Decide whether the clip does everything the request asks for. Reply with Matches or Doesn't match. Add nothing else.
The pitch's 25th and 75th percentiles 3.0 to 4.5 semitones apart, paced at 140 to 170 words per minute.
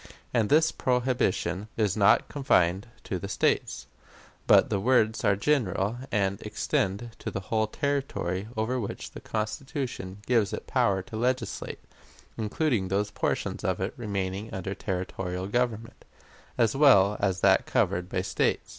Matches